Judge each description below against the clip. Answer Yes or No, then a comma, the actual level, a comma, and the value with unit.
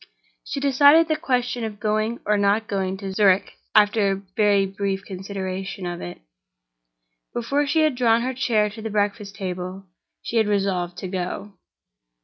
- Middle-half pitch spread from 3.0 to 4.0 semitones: Yes, average, 3.3 semitones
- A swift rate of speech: No, average, 160 wpm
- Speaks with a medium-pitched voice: No, high, 205 Hz